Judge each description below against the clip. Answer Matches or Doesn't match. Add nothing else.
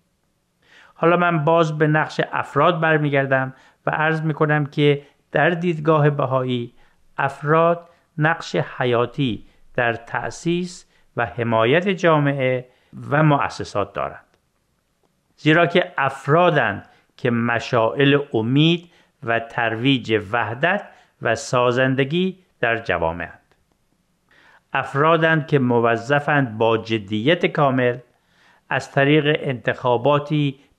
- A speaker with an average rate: Doesn't match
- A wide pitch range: Doesn't match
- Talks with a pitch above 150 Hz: Doesn't match